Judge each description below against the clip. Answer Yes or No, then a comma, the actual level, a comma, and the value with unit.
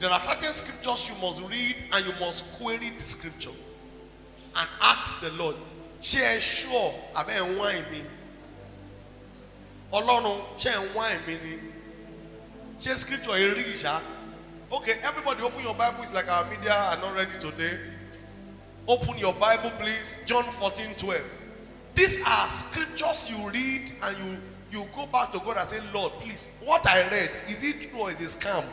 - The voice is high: Yes, high, 210 Hz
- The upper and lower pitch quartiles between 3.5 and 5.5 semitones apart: Yes, average, 4.7 semitones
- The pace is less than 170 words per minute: Yes, average, 145 wpm